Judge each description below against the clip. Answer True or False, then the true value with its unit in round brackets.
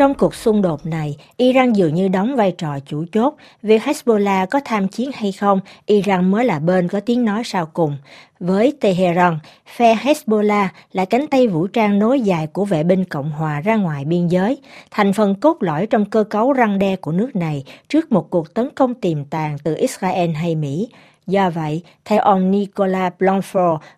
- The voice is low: False (195 Hz)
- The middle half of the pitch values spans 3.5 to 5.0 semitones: True (4.5 semitones)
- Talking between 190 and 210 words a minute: True (195 wpm)